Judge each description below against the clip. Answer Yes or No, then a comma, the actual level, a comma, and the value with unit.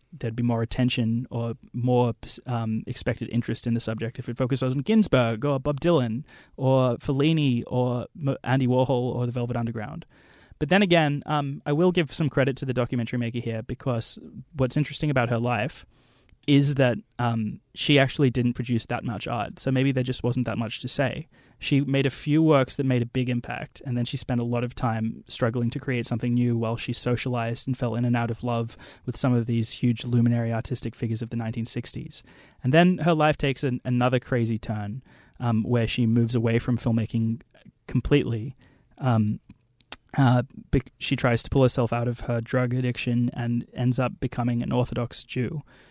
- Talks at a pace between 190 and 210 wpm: Yes, average, 195 wpm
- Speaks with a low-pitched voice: Yes, low, 125 Hz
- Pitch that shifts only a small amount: Yes, narrow, 2.2 semitones